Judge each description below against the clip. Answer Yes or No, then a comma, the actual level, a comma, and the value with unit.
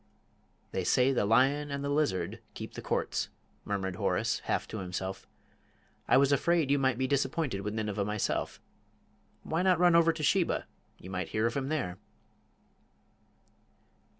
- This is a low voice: Yes, low, 130 Hz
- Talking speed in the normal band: Yes, average, 160 wpm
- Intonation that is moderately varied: No, wide, 6.4 semitones